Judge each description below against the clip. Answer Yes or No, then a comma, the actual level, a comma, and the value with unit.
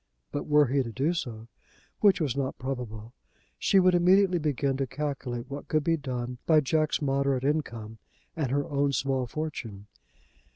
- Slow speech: No, average, 165 wpm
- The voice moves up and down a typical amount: Yes, average, 3.6 semitones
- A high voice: No, medium, 140 Hz